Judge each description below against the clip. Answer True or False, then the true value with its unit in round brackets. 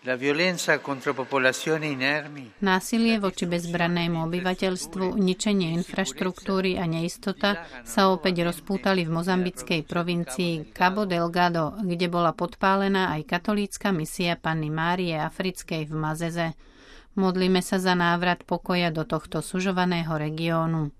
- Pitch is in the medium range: True (175 Hz)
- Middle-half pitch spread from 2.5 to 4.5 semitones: True (2.8 semitones)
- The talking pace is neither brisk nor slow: False (105 wpm)